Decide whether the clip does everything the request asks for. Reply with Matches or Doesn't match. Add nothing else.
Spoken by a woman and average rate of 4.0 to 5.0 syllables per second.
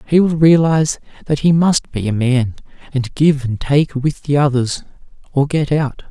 Doesn't match